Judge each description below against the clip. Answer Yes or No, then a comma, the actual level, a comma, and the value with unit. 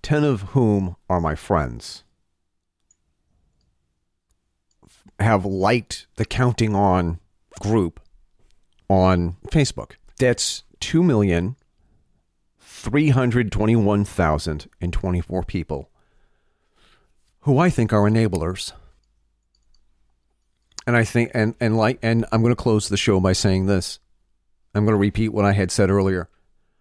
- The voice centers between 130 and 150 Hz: No, very low, 95 Hz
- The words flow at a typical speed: No, slow, 125 wpm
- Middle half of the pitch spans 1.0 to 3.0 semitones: No, average, 4.5 semitones